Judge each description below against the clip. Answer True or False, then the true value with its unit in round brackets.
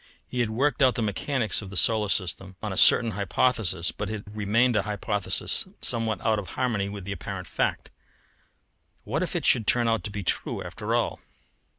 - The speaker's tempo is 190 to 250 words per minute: True (195 wpm)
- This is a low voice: True (105 Hz)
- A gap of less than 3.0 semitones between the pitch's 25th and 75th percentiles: True (2.6 semitones)